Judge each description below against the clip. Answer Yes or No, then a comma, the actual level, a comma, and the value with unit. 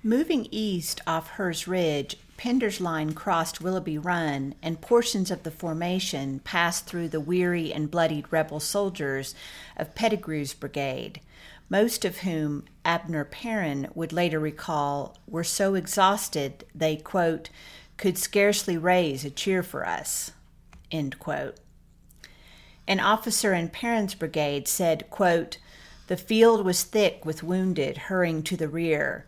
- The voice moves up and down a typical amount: Yes, average, 3.8 semitones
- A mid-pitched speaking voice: Yes, medium, 170 Hz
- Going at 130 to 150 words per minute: Yes, slow, 135 wpm